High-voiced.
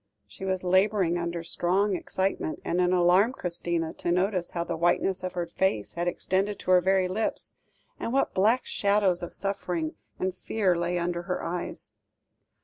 No: medium, 180 Hz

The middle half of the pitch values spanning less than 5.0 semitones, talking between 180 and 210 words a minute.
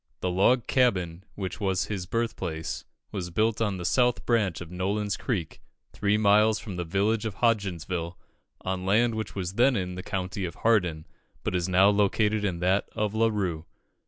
Yes: average, 3.2 semitones; average, 185 wpm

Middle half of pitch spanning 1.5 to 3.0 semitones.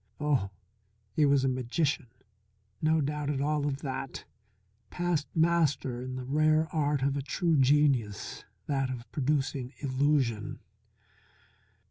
Yes: narrow, 2.5 semitones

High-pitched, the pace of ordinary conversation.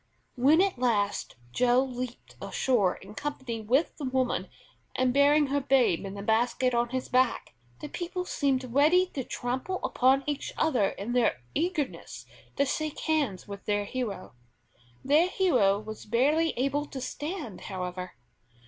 Yes: very high, 255 Hz; average, 150 wpm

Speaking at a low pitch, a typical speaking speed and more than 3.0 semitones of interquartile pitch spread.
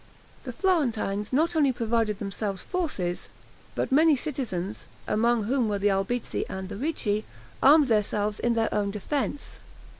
No: high, 225 Hz; average, 145 wpm; average, 5.2 semitones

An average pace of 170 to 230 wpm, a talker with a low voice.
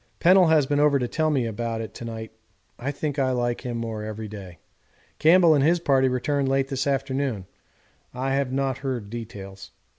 Yes: average, 200 wpm; low, 130 Hz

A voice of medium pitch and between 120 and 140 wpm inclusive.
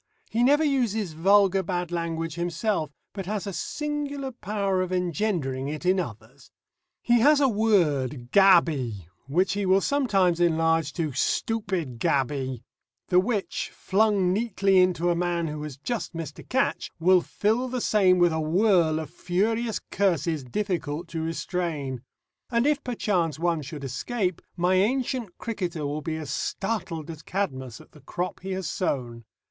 No: medium, 180 Hz; average, 155 wpm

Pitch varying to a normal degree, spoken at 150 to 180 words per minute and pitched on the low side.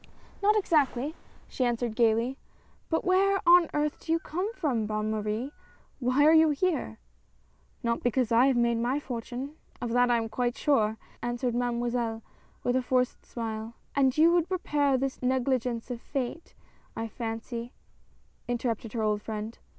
No: average, 3.8 semitones; average, 175 wpm; high, 245 Hz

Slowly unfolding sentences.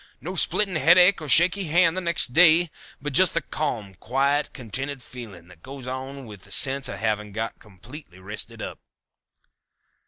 No: average, 160 wpm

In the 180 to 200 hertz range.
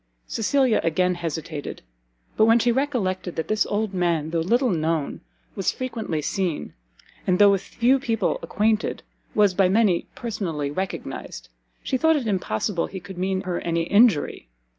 Yes: high, 190 Hz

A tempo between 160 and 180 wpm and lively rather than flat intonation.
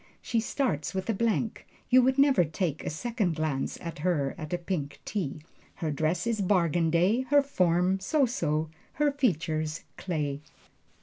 Yes: average, 165 wpm; wide, 6.5 semitones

